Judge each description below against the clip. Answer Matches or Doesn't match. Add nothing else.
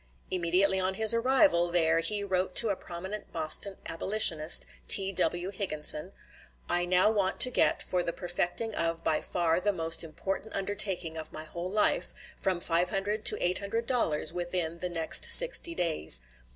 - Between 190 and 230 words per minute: Doesn't match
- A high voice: Doesn't match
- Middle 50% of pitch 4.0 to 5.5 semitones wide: Doesn't match